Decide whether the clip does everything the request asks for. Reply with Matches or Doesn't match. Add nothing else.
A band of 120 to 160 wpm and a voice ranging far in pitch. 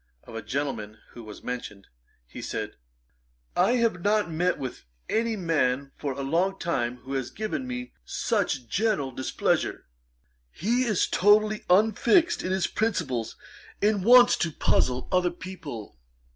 Matches